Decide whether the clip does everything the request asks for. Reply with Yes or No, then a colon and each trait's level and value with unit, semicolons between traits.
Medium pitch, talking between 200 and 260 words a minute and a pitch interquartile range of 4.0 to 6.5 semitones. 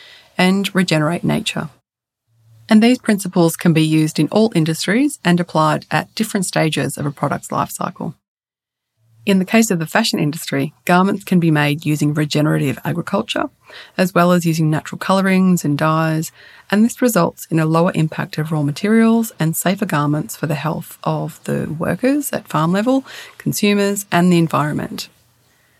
No: medium, 170 Hz; average, 165 wpm; average, 4.5 semitones